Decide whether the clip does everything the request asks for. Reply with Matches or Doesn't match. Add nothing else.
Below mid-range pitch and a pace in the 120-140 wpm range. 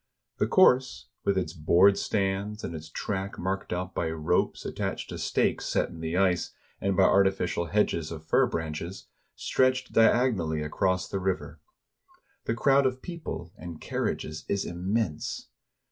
Doesn't match